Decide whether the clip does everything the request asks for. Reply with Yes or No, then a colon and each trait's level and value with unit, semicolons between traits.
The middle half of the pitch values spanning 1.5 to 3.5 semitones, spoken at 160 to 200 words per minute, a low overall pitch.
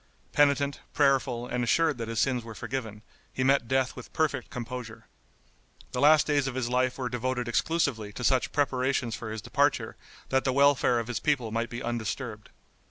Yes: average, 2.8 semitones; average, 180 wpm; low, 125 Hz